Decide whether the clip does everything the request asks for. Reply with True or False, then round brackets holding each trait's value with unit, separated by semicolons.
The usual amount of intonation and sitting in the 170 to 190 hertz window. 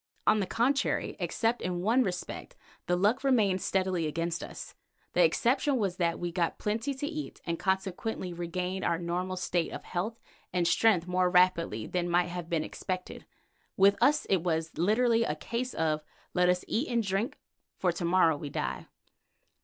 True (4.3 semitones; 185 Hz)